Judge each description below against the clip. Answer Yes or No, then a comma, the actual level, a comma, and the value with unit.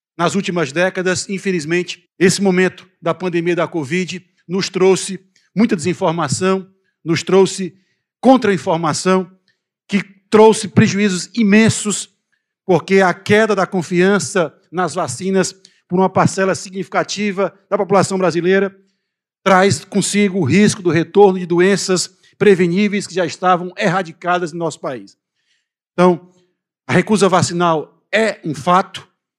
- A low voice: No, medium, 185 Hz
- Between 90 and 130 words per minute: Yes, slow, 120 wpm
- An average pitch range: No, narrow, 1.8 semitones